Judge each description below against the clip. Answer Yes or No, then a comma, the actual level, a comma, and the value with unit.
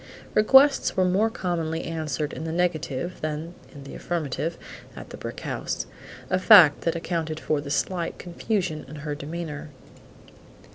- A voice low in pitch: No, medium, 165 Hz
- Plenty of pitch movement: No, average, 2.9 semitones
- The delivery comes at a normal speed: Yes, average, 150 wpm